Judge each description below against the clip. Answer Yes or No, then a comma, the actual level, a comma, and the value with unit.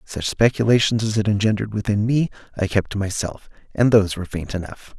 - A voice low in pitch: Yes, low, 105 Hz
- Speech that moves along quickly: No, average, 190 wpm